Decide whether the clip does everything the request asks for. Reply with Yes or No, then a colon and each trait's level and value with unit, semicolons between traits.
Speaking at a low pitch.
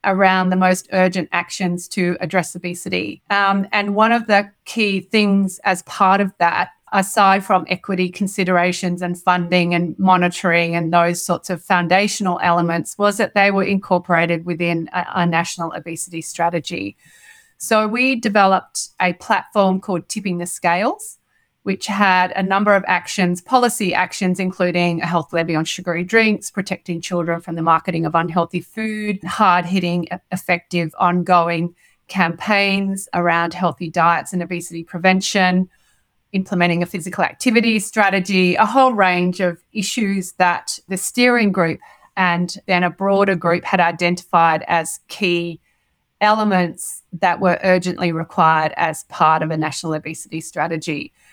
No: medium, 180 Hz